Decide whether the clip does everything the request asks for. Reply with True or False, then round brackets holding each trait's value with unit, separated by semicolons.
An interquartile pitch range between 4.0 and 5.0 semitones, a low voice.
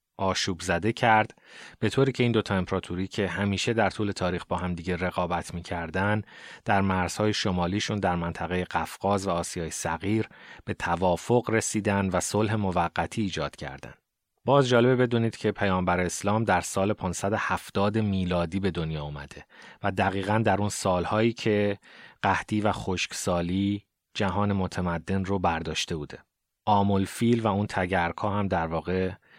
False (2.9 semitones; 95 Hz)